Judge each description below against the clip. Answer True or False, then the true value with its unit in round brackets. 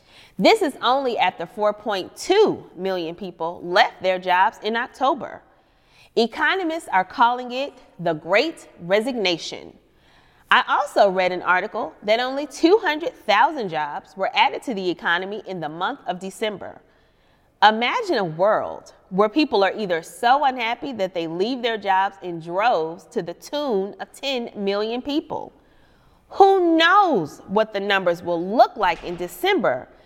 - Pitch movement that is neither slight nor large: False (7.6 semitones)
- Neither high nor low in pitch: False (210 Hz)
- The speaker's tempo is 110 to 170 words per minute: True (140 wpm)